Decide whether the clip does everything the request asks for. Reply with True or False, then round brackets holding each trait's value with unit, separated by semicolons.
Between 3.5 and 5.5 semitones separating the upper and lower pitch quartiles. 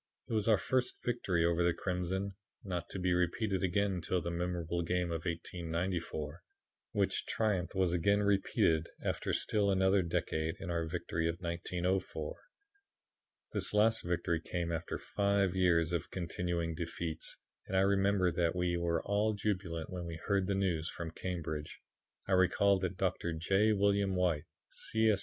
False (2.6 semitones)